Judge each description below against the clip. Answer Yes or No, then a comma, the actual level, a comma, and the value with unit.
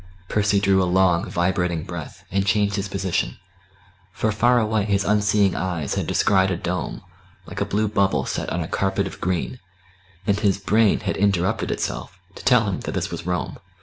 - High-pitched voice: No, very low, 95 Hz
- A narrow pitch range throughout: Yes, narrow, 2.3 semitones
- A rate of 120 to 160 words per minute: No, average, 185 wpm